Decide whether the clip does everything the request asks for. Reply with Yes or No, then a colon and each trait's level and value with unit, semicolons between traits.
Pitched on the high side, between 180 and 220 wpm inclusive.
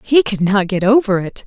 No: high, 215 Hz; fast, 245 wpm